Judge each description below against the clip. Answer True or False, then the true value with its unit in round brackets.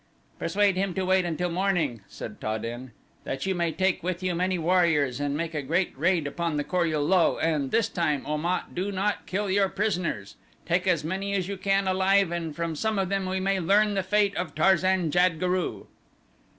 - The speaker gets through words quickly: True (210 wpm)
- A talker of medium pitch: True (180 Hz)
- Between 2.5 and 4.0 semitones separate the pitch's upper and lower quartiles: True (3.1 semitones)